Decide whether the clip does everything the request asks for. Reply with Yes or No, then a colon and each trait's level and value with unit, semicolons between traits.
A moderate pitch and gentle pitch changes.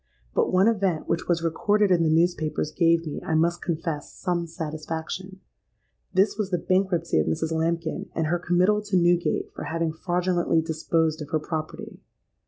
Yes: medium, 170 Hz; narrow, 2.3 semitones